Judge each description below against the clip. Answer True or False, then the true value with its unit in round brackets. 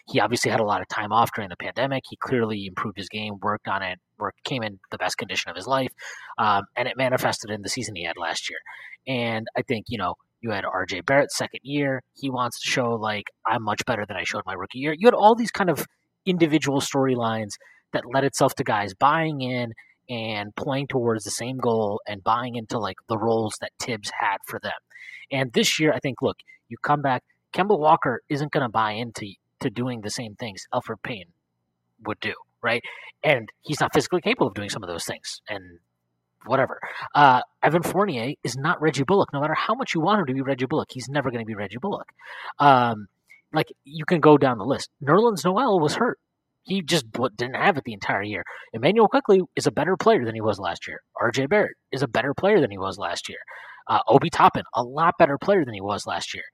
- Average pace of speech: False (225 wpm)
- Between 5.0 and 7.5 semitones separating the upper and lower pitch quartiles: True (5.6 semitones)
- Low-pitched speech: True (130 Hz)